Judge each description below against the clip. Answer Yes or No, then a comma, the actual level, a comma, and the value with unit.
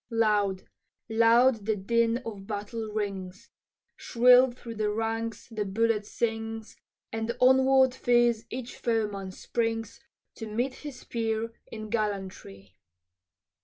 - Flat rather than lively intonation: Yes, narrow, 2.1 semitones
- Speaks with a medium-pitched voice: No, high, 225 Hz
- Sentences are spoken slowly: Yes, slow, 115 wpm